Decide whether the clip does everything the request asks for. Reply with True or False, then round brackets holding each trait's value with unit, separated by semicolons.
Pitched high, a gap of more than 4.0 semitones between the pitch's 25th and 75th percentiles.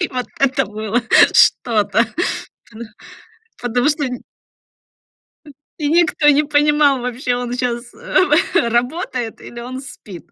False (250 Hz; 3.7 semitones)